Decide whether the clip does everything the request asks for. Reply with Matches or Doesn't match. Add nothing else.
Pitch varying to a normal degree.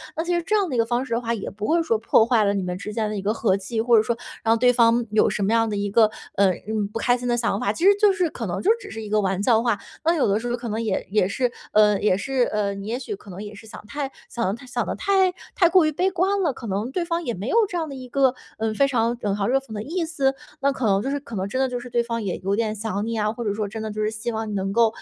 Matches